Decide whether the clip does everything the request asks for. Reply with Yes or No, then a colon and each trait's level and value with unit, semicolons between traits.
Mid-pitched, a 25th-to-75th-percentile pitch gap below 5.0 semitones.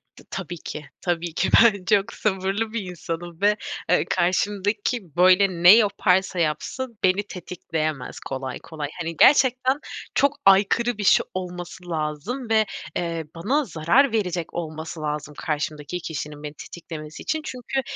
Yes: medium, 180 Hz; average, 4.6 semitones